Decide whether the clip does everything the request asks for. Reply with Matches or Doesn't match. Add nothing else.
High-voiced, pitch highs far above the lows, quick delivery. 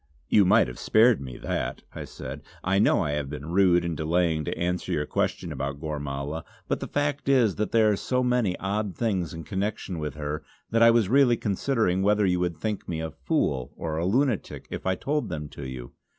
Doesn't match